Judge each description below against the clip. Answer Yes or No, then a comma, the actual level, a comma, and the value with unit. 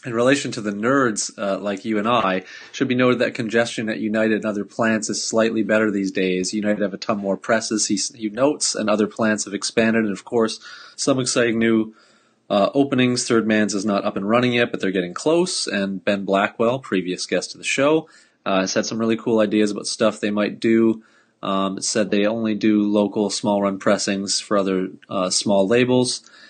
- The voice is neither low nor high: No, low, 110 Hz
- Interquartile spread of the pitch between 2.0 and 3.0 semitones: Yes, narrow, 2.5 semitones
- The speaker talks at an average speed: No, fast, 210 wpm